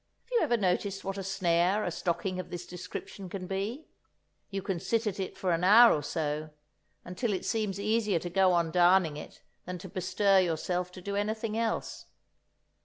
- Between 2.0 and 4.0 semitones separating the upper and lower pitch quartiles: Yes, narrow, 2.6 semitones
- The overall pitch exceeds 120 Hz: Yes, high, 190 Hz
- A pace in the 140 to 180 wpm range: No, average, 190 wpm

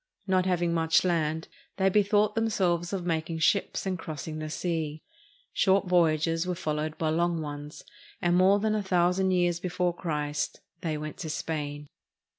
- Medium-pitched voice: Yes, medium, 170 Hz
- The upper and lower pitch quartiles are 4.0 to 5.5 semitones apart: No, average, 2.9 semitones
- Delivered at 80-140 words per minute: No, average, 175 wpm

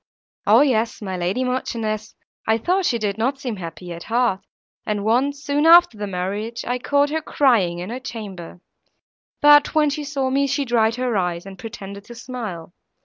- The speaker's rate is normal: Yes, average, 185 wpm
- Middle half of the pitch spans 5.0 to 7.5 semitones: Yes, average, 5.3 semitones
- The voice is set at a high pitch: Yes, high, 230 Hz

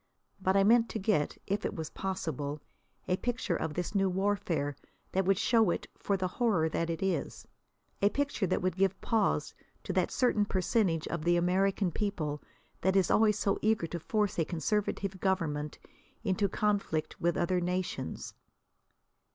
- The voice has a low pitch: No, high, 190 Hz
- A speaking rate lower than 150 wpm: No, average, 165 wpm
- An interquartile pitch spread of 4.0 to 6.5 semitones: No, average, 3.2 semitones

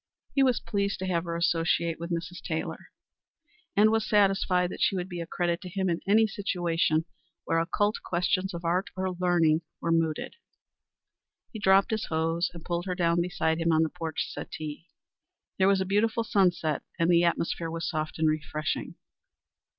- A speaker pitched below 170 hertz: No, medium, 175 Hz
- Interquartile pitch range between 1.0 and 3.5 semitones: Yes, narrow, 2.6 semitones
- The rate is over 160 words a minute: Yes, average, 180 wpm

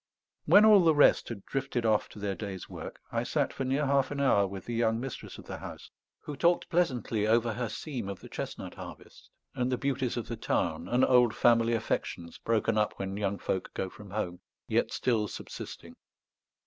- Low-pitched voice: Yes, low, 115 Hz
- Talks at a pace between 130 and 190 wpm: No, average, 200 wpm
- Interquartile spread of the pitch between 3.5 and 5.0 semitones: Yes, average, 4.4 semitones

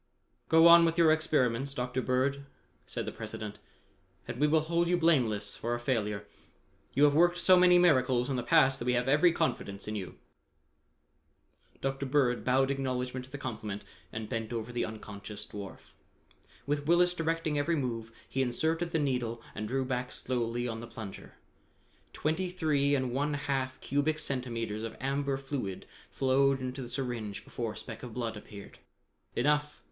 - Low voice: Yes, low, 130 Hz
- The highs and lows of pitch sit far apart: No, average, 4.1 semitones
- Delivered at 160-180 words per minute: Yes, average, 170 wpm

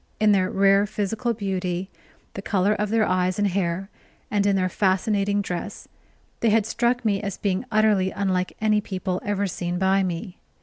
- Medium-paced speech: Yes, average, 175 wpm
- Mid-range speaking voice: No, high, 195 Hz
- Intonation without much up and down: Yes, narrow, 2.2 semitones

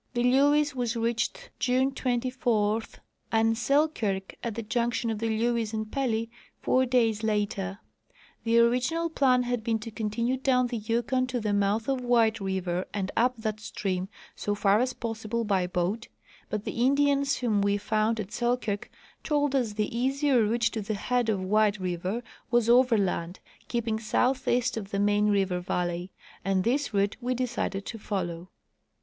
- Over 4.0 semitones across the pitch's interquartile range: No, average, 3.3 semitones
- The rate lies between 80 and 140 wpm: No, average, 165 wpm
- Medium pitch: No, high, 225 Hz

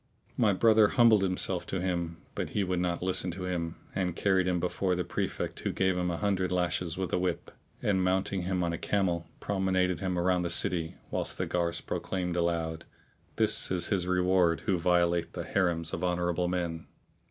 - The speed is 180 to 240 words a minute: Yes, average, 195 wpm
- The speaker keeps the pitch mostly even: Yes, narrow, 1.5 semitones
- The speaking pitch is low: Yes, very low, 90 Hz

